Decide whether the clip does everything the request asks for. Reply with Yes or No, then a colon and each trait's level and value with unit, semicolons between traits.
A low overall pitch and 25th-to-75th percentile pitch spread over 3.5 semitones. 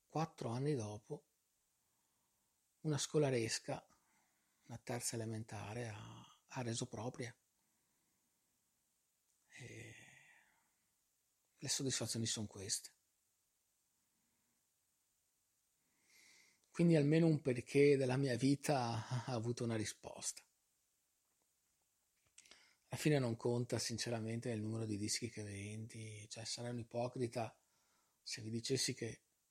No: low, 120 Hz; average, 2.8 semitones